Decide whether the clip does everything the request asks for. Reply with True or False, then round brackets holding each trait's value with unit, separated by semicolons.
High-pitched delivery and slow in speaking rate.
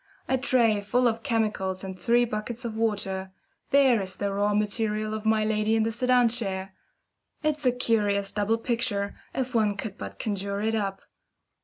False (215 Hz; 175 wpm)